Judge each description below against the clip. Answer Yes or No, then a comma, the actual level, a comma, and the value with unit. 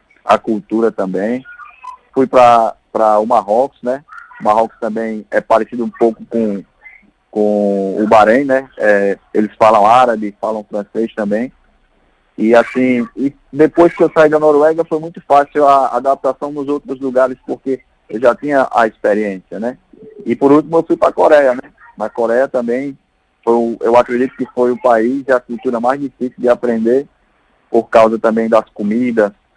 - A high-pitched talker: No, low, 120 Hz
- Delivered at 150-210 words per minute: Yes, average, 165 wpm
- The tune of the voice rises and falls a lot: No, average, 3.6 semitones